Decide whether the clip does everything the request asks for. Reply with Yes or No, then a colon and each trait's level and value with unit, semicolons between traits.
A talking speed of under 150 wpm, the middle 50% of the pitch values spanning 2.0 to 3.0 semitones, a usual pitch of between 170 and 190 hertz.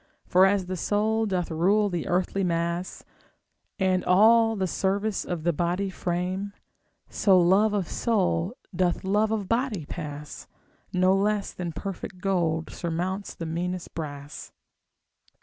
Yes: slow, 135 wpm; average, 2.7 semitones; medium, 185 Hz